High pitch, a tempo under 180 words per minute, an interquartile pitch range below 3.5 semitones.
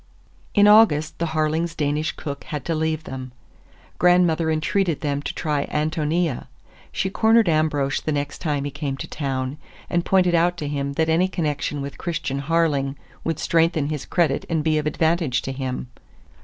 No: medium, 155 Hz; average, 170 wpm; average, 2.8 semitones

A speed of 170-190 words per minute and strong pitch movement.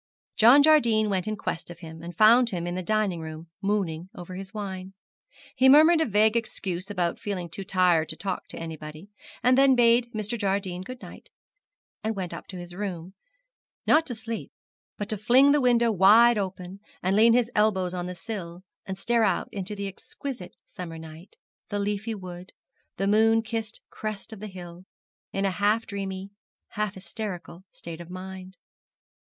No: average, 180 wpm; average, 3.5 semitones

